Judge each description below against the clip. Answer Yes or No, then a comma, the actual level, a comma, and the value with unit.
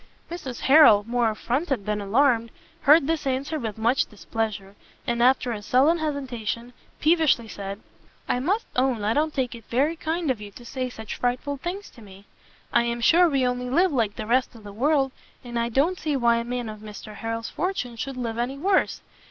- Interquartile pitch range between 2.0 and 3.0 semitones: No, average, 4.0 semitones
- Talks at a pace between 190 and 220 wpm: Yes, average, 200 wpm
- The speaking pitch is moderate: No, very high, 250 Hz